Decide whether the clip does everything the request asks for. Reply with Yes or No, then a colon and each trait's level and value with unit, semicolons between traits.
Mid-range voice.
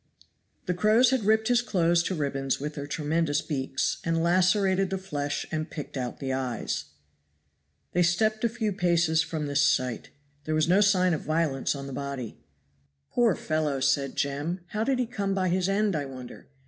Yes: medium, 165 Hz